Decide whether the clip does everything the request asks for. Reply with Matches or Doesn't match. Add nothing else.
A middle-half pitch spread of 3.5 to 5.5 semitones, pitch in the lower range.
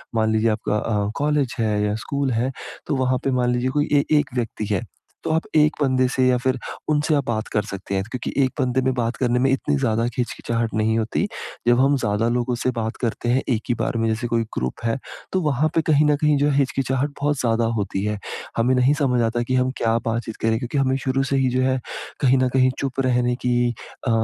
Doesn't match